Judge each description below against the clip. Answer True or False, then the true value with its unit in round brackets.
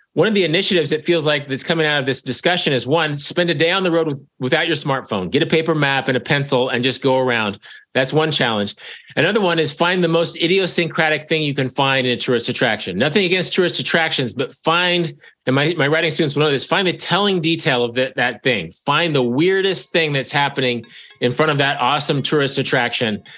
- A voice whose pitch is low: False (150 Hz)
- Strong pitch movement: False (4.0 semitones)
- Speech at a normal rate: False (230 wpm)